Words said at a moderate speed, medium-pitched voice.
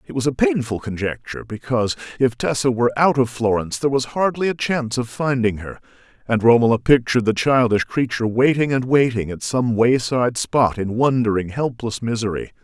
No: average, 175 wpm; low, 120 Hz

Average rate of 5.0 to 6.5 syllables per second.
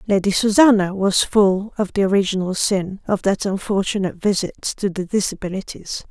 Yes: 5.1 syllables/s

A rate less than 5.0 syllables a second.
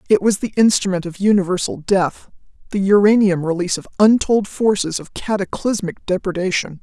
No: 5.4 syllables/s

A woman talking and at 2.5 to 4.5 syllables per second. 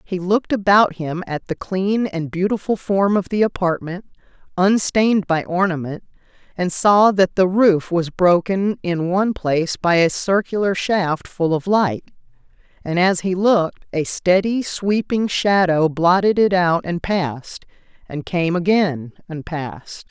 Yes: female; 4.2 syllables/s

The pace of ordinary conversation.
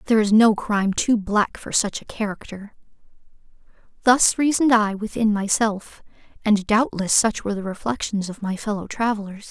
Yes: average, 160 wpm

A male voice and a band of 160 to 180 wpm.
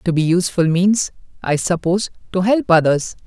Yes: male; average, 165 wpm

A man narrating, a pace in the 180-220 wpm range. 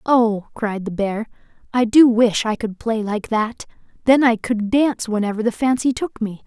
No: female; average, 195 wpm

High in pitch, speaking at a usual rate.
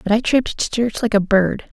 No: high, 220 Hz; fast, 265 wpm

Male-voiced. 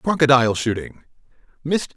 Yes: male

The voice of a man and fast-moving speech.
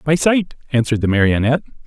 No: male; average, 160 wpm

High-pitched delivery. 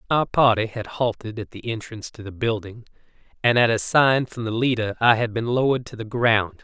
No: low, 115 Hz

